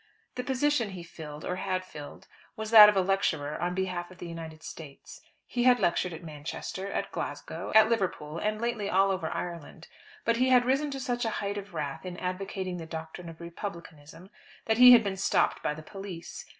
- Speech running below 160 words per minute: No, average, 200 wpm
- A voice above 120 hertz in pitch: Yes, medium, 185 Hz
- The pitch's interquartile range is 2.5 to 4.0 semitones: No, average, 4.7 semitones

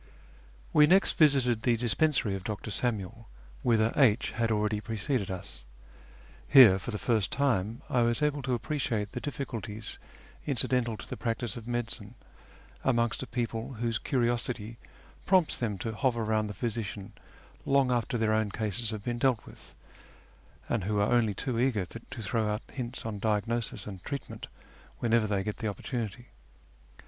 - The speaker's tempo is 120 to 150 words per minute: No, average, 160 wpm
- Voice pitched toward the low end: Yes, low, 115 Hz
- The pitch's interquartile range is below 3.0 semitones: Yes, narrow, 2.6 semitones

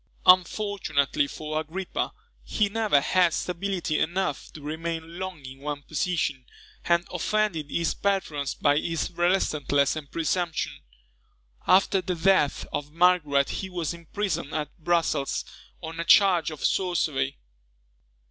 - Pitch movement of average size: Yes, average, 3.7 semitones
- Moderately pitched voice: Yes, medium, 165 Hz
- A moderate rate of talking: No, slow, 125 wpm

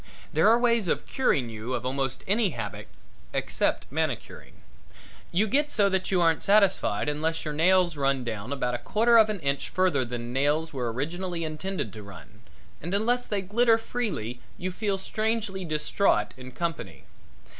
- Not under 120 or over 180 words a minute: Yes, average, 165 wpm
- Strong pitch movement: Yes, wide, 7.4 semitones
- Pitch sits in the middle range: Yes, medium, 170 Hz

